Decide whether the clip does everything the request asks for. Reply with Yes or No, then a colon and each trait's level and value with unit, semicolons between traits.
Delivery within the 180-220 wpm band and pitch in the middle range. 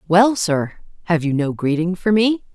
No: average, 165 wpm; medium, 180 Hz